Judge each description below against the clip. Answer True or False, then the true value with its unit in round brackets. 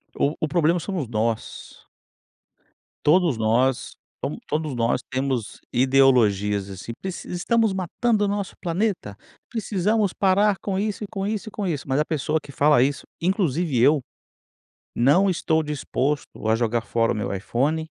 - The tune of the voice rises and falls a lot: True (7.5 semitones)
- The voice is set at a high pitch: False (150 Hz)